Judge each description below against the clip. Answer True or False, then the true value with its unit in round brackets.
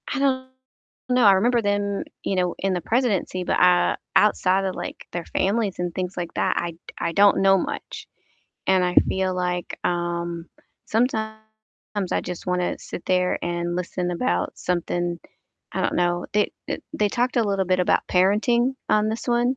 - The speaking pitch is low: False (185 Hz)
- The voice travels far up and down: False (3.2 semitones)